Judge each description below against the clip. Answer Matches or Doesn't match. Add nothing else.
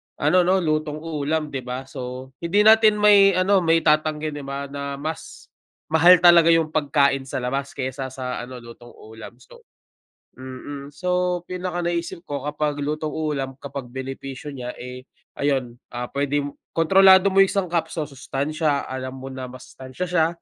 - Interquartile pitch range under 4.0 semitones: Doesn't match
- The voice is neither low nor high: Matches